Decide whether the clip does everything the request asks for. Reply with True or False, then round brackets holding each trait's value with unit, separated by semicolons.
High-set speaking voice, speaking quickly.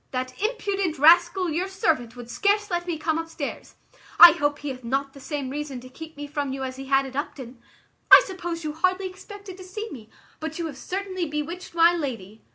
True (315 Hz; 210 wpm)